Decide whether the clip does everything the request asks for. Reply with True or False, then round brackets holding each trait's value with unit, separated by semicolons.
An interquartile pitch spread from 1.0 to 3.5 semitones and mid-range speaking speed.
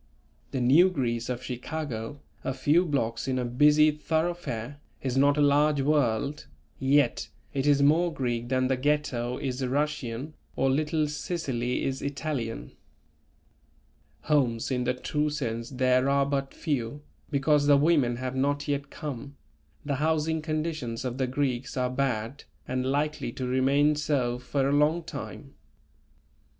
True (2.9 semitones; 145 wpm)